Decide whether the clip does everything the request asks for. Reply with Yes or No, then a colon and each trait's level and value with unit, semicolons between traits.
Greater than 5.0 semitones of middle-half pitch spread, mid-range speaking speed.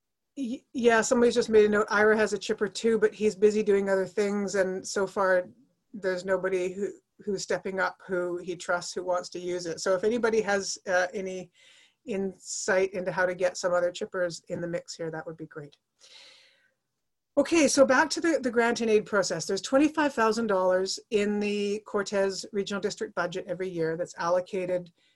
No: average, 3.4 semitones; average, 195 wpm